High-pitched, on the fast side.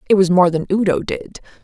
Yes: high, 200 Hz; fast, 220 wpm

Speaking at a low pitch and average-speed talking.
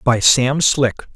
Yes: low, 130 Hz; average, 155 wpm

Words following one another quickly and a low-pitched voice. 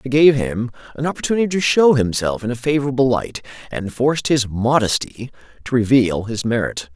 No: average, 175 wpm; low, 125 Hz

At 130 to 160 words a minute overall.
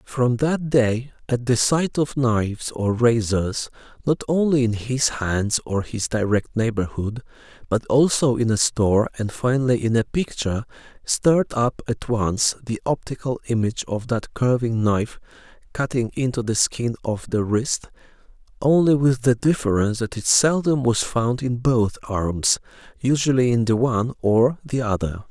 Yes: average, 155 wpm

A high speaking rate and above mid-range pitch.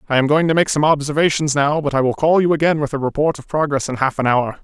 No: fast, 300 wpm; medium, 145 Hz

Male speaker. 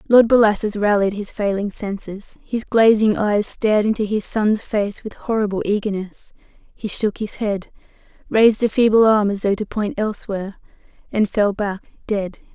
No: female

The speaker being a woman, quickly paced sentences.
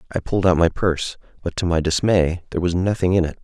No: male; fast, 245 wpm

